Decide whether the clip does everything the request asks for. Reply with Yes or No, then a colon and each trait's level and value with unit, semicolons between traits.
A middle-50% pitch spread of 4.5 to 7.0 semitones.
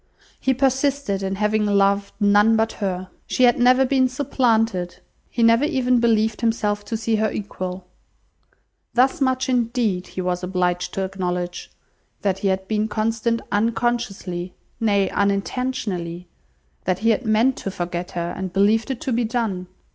No: average, 4.1 semitones